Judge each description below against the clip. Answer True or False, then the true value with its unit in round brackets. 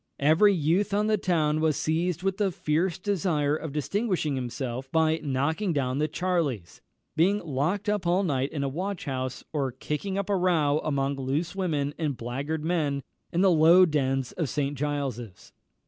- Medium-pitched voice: True (155 Hz)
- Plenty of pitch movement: False (4.6 semitones)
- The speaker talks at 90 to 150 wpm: False (175 wpm)